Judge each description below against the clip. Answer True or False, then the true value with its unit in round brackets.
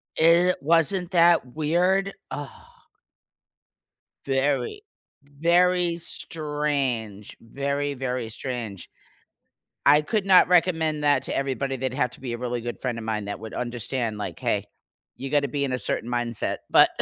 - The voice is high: False (140 Hz)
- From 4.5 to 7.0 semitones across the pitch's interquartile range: True (5.2 semitones)